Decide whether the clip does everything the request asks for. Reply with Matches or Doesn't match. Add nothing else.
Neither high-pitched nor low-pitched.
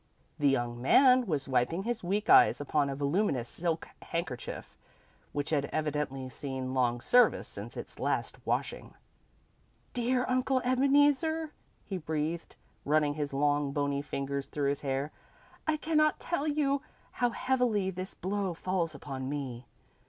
Matches